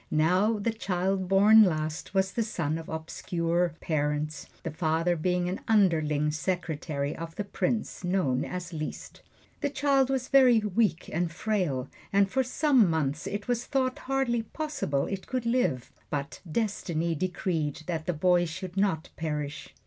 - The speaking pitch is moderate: Yes, medium, 180 Hz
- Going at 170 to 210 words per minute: No, average, 155 wpm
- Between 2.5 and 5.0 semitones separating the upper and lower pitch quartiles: No, wide, 5.4 semitones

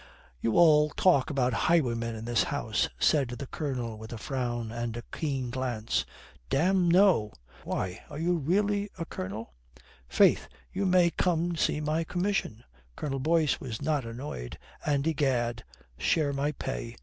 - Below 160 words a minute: Yes, average, 150 wpm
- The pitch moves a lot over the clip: Yes, wide, 5.8 semitones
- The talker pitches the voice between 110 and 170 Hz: Yes, medium, 140 Hz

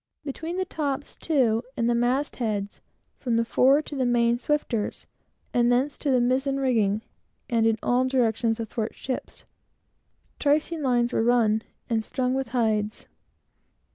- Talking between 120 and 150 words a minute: Yes, average, 145 wpm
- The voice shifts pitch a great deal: No, average, 3.0 semitones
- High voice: Yes, high, 245 Hz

